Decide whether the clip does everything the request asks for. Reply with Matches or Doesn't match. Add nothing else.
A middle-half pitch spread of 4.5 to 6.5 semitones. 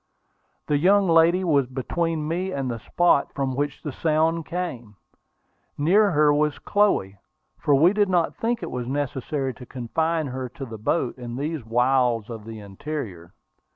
Matches